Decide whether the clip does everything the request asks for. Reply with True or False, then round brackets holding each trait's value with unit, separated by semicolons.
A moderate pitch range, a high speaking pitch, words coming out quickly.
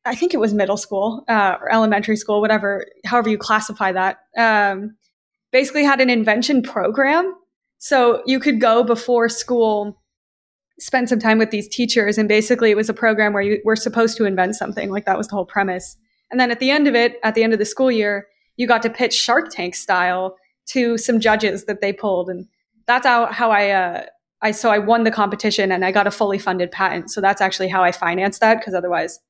True (3.0 semitones; 215 Hz; 220 wpm)